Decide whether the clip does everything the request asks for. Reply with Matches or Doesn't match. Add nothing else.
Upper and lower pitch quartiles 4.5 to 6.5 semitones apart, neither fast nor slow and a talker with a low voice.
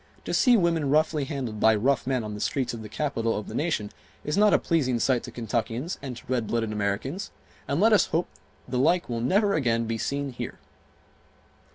Doesn't match